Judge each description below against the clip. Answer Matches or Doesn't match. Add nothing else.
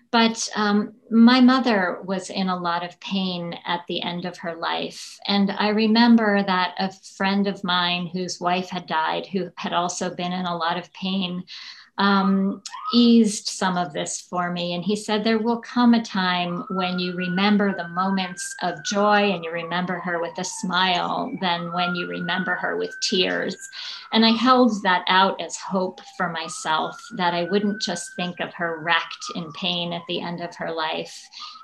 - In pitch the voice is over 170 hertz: Matches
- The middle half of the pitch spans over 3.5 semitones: Doesn't match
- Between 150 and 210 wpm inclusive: Matches